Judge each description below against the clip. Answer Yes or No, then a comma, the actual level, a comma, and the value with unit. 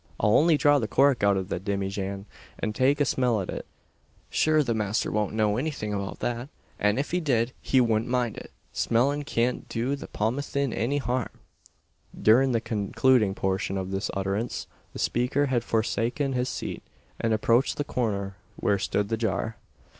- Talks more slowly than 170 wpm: No, average, 175 wpm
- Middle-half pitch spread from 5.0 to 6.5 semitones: No, average, 4.2 semitones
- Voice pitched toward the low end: Yes, low, 115 Hz